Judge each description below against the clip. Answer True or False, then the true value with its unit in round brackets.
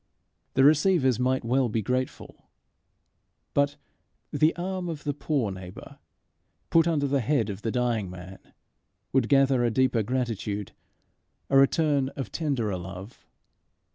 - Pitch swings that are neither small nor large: True (4.5 semitones)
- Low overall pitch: True (130 Hz)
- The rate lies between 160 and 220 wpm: False (135 wpm)